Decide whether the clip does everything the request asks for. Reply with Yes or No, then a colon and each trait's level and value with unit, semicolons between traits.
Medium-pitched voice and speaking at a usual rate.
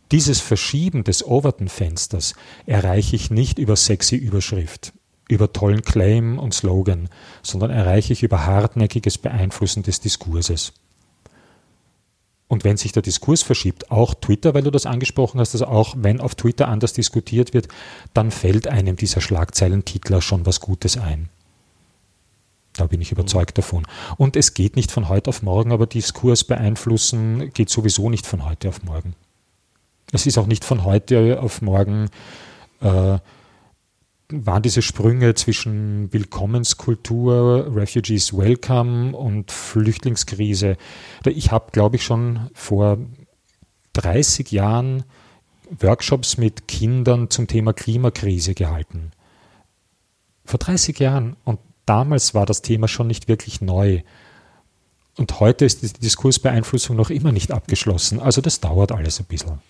No: low, 110 Hz; average, 135 wpm